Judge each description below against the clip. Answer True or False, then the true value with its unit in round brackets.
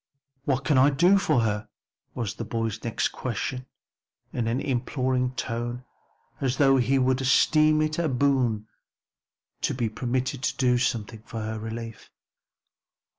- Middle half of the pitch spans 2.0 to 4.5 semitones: True (2.8 semitones)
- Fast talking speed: False (145 wpm)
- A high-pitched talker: False (125 Hz)